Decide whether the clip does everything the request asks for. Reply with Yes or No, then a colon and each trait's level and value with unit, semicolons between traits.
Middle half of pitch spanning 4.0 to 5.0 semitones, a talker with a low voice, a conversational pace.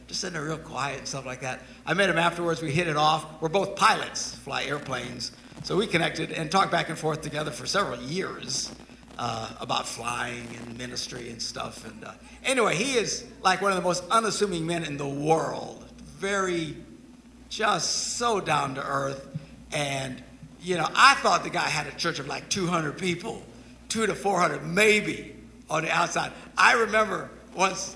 No: average, 4.7 semitones; medium, 170 Hz; average, 185 wpm